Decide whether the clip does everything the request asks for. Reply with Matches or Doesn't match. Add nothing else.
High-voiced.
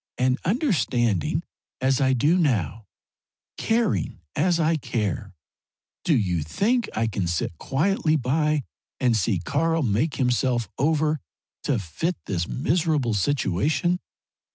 Doesn't match